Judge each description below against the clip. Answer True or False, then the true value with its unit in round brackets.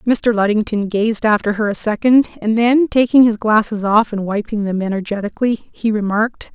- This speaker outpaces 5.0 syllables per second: True (5.3 syllables/s)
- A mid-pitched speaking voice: False (215 Hz)